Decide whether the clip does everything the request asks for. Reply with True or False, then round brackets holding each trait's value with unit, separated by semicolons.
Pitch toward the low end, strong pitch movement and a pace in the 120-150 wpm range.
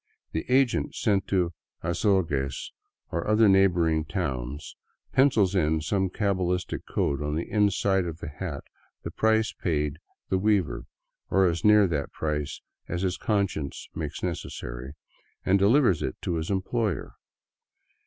False (90 Hz; 4.4 semitones; 145 wpm)